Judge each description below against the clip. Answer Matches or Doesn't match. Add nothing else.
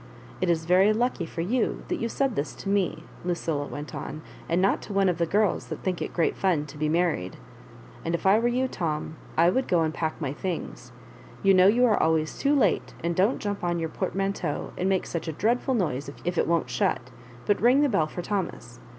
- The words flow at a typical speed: Doesn't match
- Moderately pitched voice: Matches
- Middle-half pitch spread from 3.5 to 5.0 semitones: Matches